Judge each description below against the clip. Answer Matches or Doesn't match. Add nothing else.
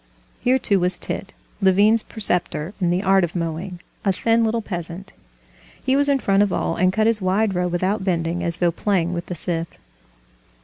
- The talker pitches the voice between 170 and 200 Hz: Matches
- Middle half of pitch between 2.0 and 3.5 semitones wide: Matches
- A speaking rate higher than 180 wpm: Matches